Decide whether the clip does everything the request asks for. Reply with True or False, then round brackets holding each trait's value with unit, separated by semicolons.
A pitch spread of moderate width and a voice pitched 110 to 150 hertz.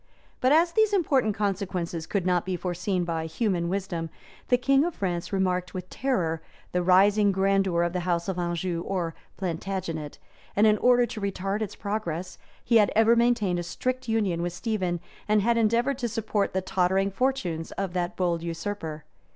False (3.8 semitones; 190 Hz)